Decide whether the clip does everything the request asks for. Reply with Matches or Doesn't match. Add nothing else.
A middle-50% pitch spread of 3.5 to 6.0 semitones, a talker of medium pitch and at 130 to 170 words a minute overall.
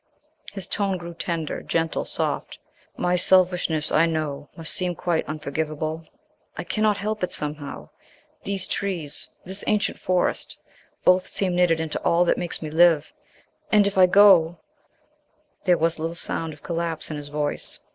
Doesn't match